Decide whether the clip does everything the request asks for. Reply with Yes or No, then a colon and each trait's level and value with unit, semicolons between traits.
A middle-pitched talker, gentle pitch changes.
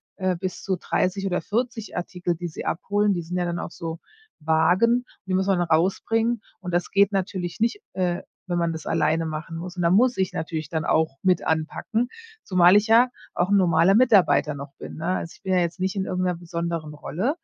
No: medium, 180 Hz; average, 3.0 semitones